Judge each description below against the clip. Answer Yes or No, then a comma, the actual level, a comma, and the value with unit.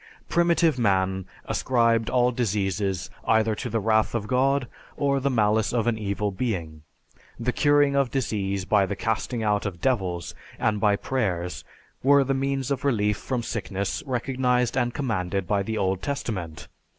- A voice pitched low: Yes, low, 110 Hz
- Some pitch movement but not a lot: Yes, average, 4.5 semitones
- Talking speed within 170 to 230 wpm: No, average, 160 wpm